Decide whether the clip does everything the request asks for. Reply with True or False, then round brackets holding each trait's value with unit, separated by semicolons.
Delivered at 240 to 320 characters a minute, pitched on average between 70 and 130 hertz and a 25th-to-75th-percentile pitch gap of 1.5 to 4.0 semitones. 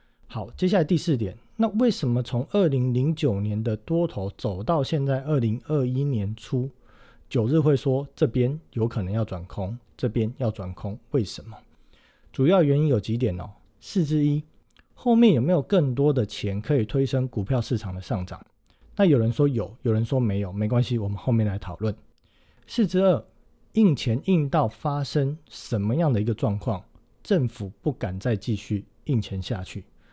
False (255 characters per minute; 125 Hz; 5.6 semitones)